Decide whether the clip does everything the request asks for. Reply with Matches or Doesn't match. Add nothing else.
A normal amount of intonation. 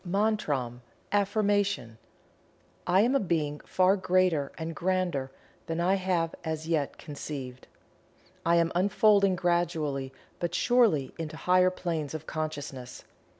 Matches